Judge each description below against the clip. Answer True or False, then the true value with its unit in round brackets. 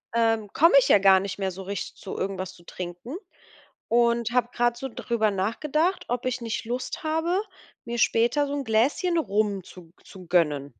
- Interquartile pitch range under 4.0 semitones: False (4.8 semitones)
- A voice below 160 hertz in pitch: False (225 Hz)